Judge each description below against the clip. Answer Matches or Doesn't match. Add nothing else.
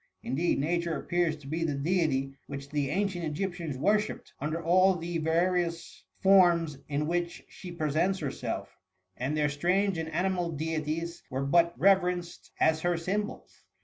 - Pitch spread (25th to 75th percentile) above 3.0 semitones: Doesn't match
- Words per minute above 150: Matches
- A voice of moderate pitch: Matches